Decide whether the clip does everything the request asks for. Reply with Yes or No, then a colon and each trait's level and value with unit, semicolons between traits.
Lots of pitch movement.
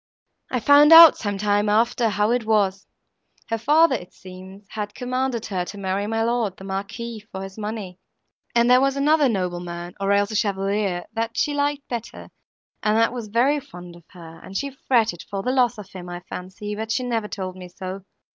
No: average, 4.0 semitones